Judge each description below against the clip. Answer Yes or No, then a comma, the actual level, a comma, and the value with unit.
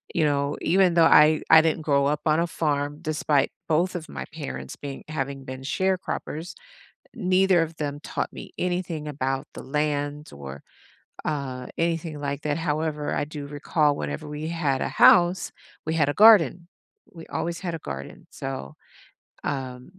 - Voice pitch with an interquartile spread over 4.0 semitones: No, average, 2.8 semitones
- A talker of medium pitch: Yes, medium, 150 Hz